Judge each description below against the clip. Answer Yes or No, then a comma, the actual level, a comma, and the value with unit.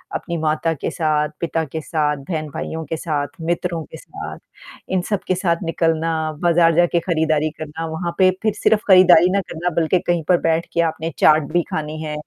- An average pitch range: No, narrow, 1.9 semitones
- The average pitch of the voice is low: No, medium, 165 Hz